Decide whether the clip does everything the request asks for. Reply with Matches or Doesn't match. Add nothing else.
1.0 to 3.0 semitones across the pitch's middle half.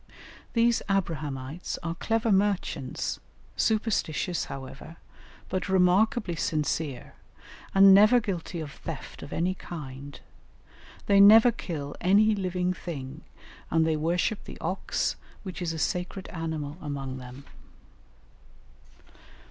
Doesn't match